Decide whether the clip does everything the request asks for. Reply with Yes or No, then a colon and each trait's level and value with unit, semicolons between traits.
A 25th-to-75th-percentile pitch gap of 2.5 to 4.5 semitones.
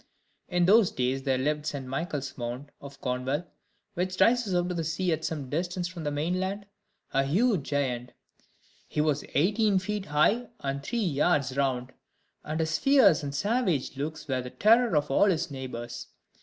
No: average, 5.3 semitones